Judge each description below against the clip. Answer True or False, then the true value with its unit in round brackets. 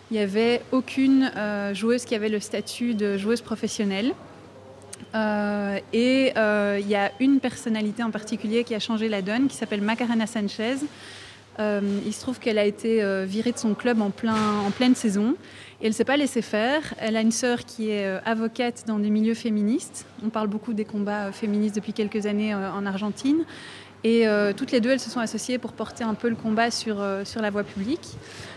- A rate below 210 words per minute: False (215 wpm)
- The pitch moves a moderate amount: False (2.2 semitones)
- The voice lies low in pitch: False (220 Hz)